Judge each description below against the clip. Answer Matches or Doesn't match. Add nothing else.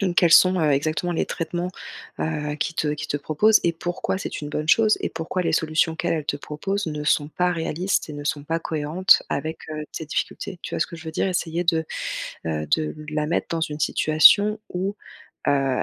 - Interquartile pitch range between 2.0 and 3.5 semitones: Matches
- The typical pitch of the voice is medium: Matches